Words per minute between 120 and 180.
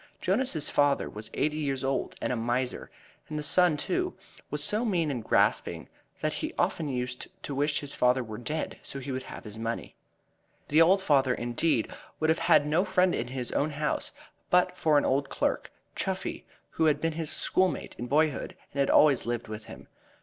No: average, 195 wpm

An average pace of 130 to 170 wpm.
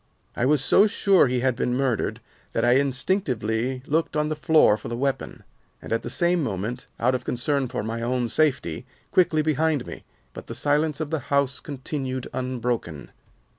No: average, 180 wpm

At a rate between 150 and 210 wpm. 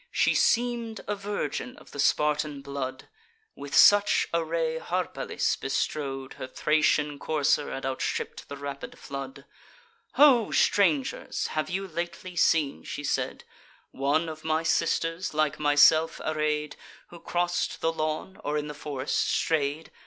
No: slow, 135 wpm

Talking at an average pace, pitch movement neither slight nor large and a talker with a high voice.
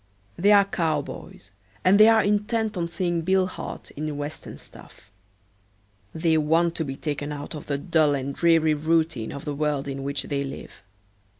No: average, 175 wpm; average, 3.3 semitones; medium, 155 Hz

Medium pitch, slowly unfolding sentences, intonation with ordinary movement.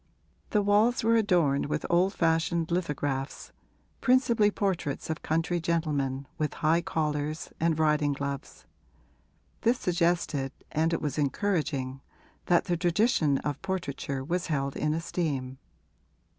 Yes: medium, 160 Hz; slow, 125 wpm; average, 3.7 semitones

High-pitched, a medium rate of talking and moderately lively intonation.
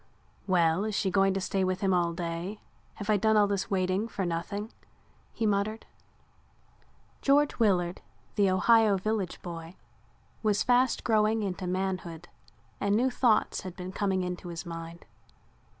Yes: high, 195 Hz; average, 150 wpm; average, 3.0 semitones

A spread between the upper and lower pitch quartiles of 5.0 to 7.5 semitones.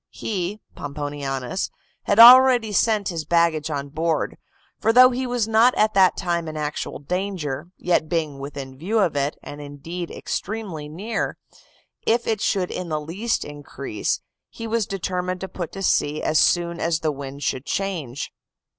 Yes: wide, 5.6 semitones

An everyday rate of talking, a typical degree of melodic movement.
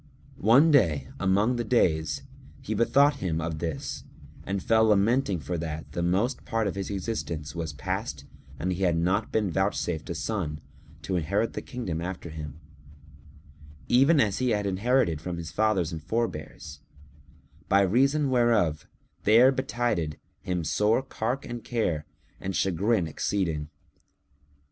No: average, 150 wpm; wide, 5.9 semitones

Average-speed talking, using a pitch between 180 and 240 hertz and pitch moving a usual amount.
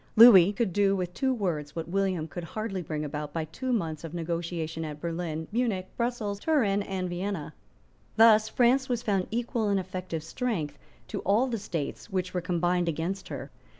Yes: average, 180 wpm; medium, 185 Hz; average, 4.6 semitones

